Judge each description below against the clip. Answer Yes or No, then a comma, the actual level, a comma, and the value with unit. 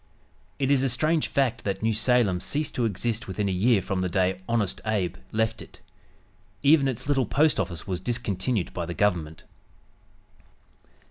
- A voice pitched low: Yes, low, 110 Hz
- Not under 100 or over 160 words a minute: No, average, 170 wpm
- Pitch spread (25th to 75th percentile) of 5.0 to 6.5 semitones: Yes, average, 5.3 semitones